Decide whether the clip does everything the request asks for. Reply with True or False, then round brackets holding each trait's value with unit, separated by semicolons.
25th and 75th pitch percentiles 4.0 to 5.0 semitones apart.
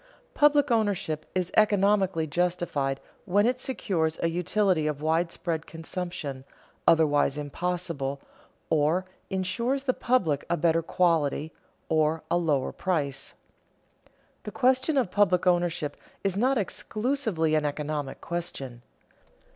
True (4.7 semitones)